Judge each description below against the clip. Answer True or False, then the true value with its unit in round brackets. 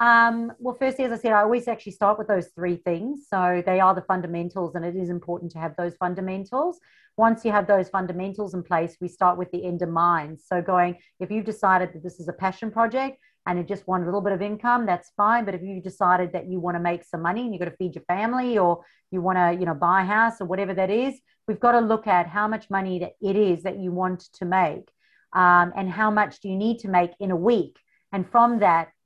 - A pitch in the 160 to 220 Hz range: True (190 Hz)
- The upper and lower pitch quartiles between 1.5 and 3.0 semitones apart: False (3.4 semitones)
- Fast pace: True (255 wpm)